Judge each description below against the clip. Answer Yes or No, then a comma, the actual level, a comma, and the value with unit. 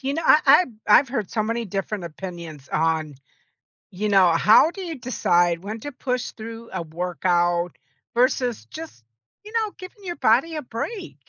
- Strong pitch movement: Yes, wide, 8.0 semitones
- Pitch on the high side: Yes, high, 220 Hz